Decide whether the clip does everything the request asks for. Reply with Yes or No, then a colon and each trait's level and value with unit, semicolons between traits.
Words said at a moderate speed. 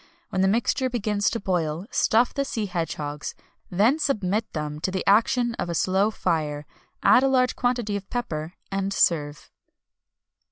Yes: average, 160 wpm